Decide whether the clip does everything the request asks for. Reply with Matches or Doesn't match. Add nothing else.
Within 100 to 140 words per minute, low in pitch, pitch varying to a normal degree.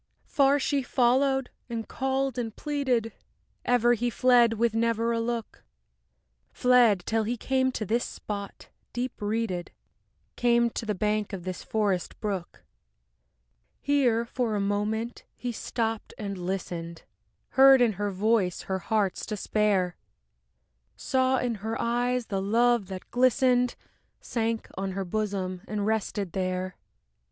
Doesn't match